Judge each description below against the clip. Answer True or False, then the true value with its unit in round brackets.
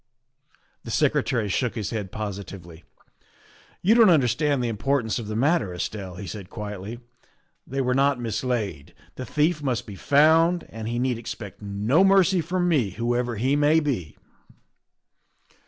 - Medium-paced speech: True (160 wpm)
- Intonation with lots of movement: True (6.0 semitones)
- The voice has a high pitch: False (120 Hz)